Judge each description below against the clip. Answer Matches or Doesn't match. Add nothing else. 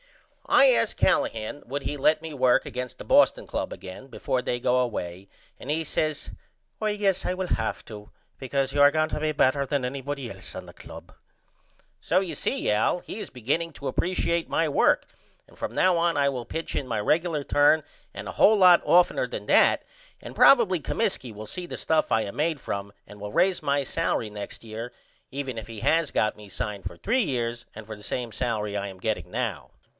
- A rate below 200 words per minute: Doesn't match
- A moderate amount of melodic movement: Doesn't match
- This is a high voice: Doesn't match